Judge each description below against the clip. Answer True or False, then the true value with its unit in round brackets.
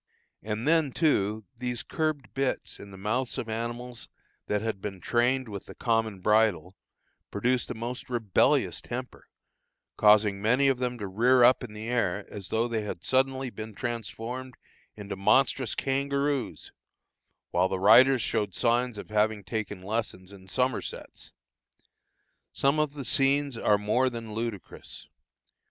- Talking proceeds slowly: False (145 wpm)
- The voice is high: False (115 Hz)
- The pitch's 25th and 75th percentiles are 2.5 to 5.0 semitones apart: True (3.6 semitones)